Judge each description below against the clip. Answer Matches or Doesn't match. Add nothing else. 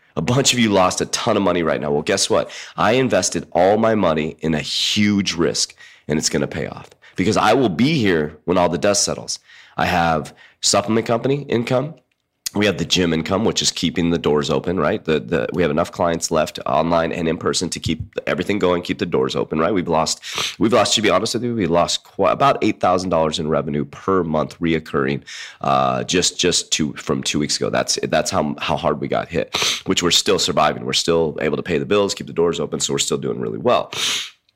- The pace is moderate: Doesn't match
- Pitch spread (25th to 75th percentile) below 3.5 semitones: Doesn't match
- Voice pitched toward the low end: Matches